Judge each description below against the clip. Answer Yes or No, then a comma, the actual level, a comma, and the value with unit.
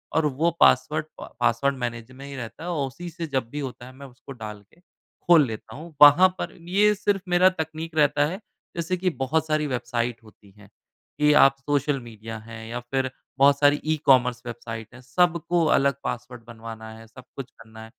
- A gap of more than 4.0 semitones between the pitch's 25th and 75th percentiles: Yes, average, 4.7 semitones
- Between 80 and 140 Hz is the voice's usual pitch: Yes, low, 135 Hz